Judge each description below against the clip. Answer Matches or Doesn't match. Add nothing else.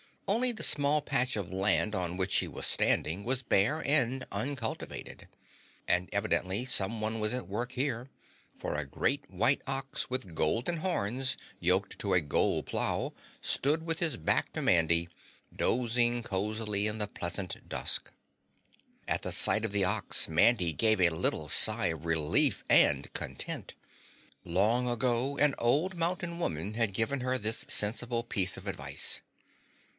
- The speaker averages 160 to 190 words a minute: Doesn't match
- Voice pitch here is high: Doesn't match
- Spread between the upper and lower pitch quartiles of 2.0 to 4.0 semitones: Doesn't match